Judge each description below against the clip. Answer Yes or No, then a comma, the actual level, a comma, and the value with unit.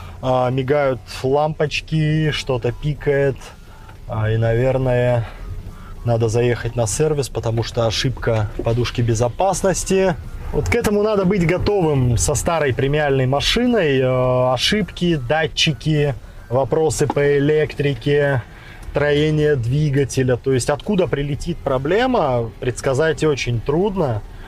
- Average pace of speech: No, slow, 100 wpm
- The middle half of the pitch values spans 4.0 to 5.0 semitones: Yes, average, 4.3 semitones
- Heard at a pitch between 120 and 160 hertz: Yes, low, 135 Hz